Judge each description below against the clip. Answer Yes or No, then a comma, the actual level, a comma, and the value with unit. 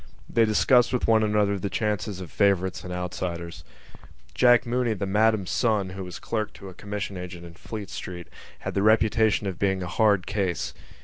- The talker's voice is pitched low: Yes, low, 100 Hz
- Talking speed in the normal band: Yes, average, 185 wpm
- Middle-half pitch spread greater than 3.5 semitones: No, average, 3.1 semitones